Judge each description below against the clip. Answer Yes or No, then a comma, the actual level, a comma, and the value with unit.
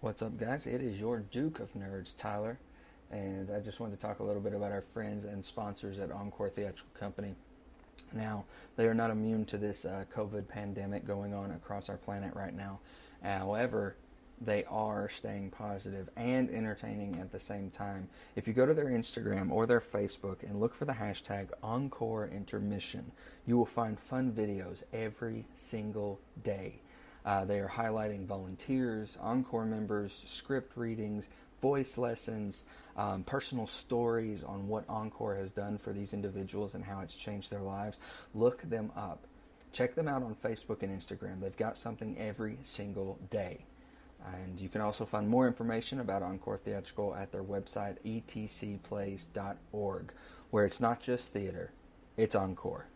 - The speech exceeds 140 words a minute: Yes, average, 165 wpm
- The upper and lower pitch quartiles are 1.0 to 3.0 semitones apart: Yes, narrow, 2.4 semitones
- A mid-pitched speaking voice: No, low, 105 Hz